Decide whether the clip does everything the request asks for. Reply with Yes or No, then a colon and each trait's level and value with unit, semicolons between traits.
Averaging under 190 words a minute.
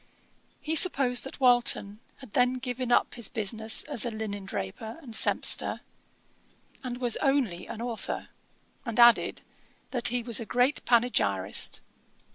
Yes: average, 140 wpm